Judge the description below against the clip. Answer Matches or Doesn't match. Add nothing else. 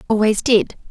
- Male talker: Doesn't match